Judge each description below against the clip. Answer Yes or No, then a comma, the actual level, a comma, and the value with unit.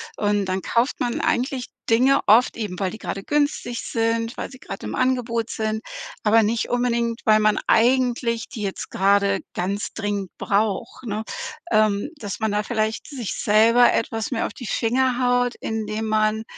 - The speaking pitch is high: Yes, high, 225 Hz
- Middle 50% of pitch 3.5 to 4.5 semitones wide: No, narrow, 2.5 semitones